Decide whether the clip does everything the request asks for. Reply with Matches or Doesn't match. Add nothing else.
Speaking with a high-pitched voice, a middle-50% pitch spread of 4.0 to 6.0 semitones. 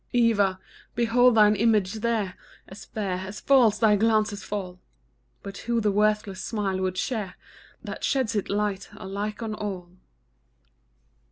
Doesn't match